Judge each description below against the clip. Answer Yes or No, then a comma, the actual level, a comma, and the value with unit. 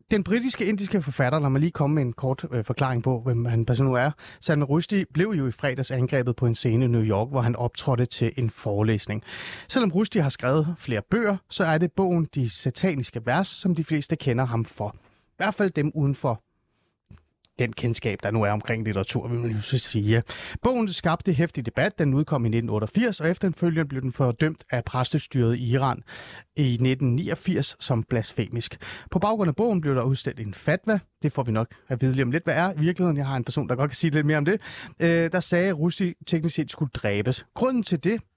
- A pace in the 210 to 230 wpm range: Yes, average, 220 wpm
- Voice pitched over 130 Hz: Yes, medium, 140 Hz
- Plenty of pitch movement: Yes, wide, 5.9 semitones